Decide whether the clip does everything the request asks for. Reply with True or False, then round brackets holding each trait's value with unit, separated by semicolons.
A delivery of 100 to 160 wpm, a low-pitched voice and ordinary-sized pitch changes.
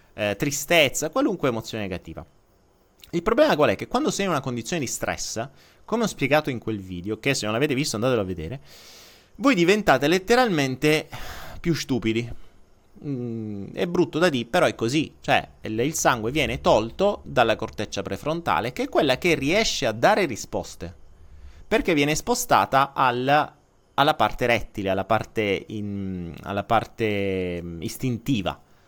False (155 wpm; 115 Hz; 7.4 semitones)